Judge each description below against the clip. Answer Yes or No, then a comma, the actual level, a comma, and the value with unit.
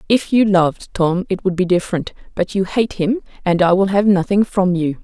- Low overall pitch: No, high, 190 Hz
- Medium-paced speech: No, fast, 225 wpm